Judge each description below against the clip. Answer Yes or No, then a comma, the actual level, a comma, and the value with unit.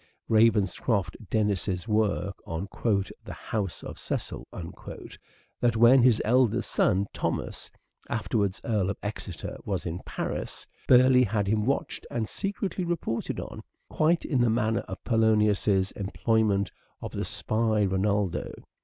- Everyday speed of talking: No, slow, 130 wpm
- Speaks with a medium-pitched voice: No, low, 110 Hz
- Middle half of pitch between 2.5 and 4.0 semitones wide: Yes, average, 2.9 semitones